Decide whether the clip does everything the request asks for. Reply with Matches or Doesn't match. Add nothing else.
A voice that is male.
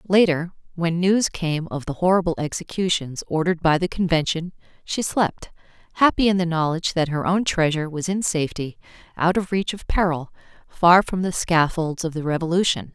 Doesn't match